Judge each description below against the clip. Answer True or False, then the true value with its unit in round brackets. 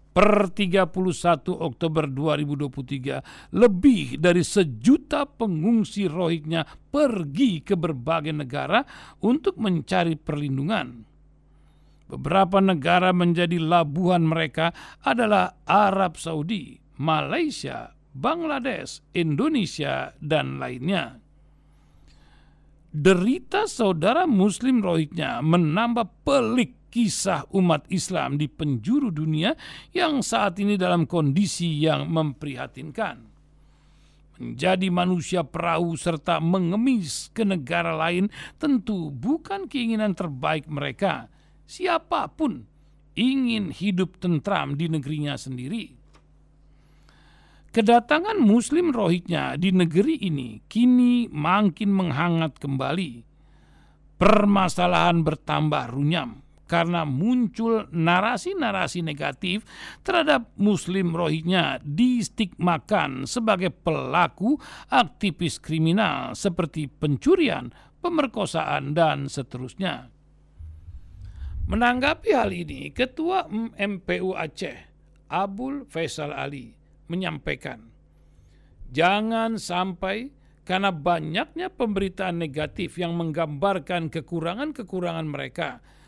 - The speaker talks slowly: True (80 wpm)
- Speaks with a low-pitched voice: False (175 Hz)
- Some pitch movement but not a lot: False (5.7 semitones)